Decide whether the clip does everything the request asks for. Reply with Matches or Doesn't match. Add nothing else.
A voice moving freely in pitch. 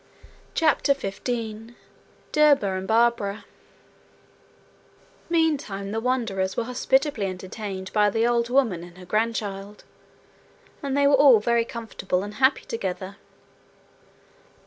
Doesn't match